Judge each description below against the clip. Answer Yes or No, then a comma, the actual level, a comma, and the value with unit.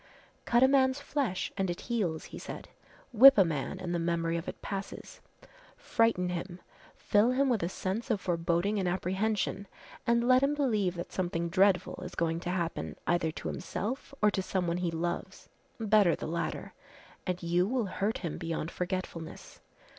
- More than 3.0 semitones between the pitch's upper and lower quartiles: Yes, average, 4.3 semitones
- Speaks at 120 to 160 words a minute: No, average, 175 wpm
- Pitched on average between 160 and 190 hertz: Yes, medium, 185 Hz